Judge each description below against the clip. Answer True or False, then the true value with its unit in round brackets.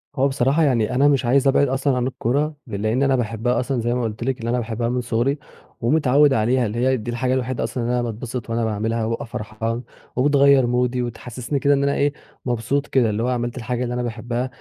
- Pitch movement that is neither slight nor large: False (2.3 semitones)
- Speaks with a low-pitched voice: True (125 Hz)